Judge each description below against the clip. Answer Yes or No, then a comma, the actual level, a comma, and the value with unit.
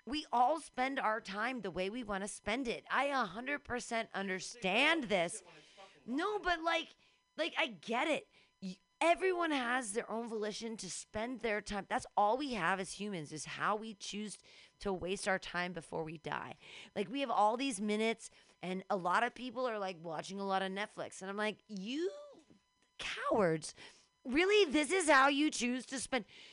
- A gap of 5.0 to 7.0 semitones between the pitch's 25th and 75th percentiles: Yes, wide, 5.5 semitones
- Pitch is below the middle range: No, high, 220 Hz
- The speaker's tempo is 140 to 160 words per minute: No, average, 180 wpm